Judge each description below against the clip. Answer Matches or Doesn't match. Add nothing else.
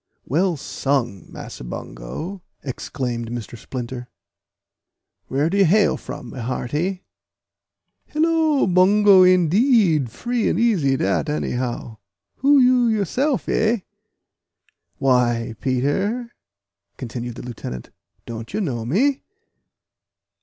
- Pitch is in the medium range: Matches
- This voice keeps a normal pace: Doesn't match